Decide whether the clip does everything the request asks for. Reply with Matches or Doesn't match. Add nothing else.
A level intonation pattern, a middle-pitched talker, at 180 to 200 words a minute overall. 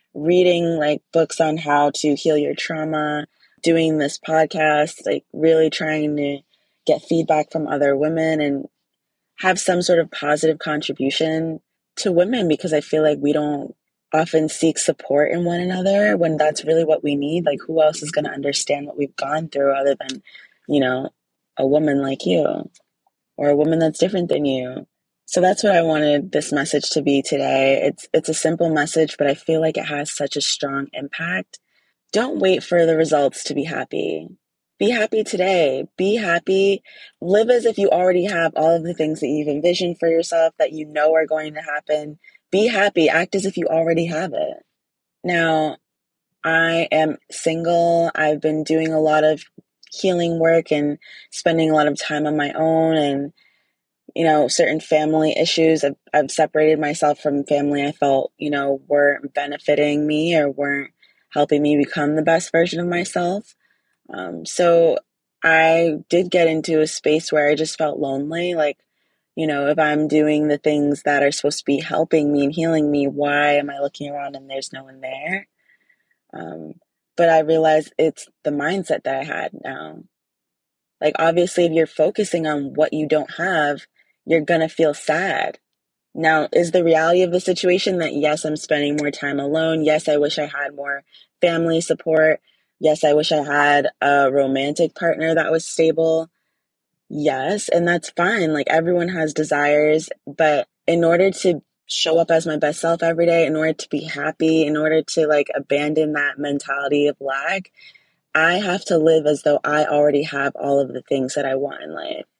Matches